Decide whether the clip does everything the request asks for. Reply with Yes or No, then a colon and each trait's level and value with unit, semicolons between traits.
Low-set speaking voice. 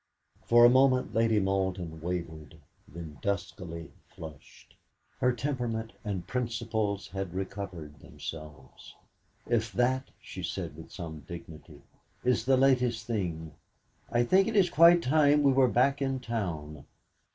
Yes: low, 105 Hz